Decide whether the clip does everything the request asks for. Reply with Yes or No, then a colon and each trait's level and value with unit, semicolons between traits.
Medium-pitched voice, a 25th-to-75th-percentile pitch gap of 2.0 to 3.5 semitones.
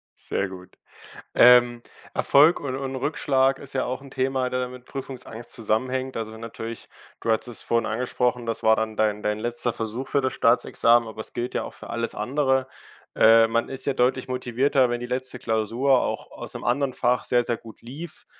No: low, 125 Hz; narrow, 2.5 semitones